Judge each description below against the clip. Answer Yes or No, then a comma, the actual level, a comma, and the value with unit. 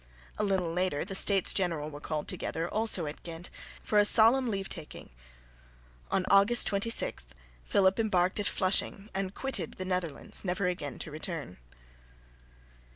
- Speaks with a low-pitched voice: No, medium, 185 Hz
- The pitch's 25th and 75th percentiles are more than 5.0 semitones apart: No, average, 3.6 semitones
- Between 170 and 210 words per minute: No, average, 150 wpm